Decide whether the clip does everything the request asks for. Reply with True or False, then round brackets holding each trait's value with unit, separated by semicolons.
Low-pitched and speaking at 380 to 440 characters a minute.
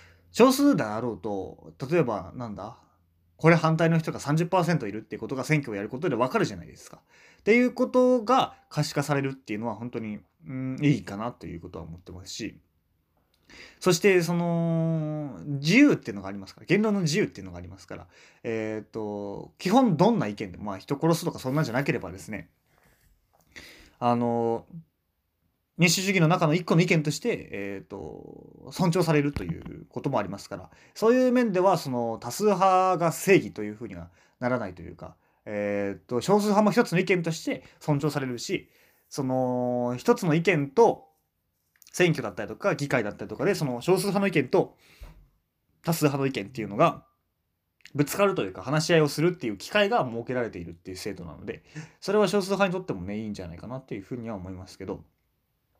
True (130 Hz; 390 characters per minute)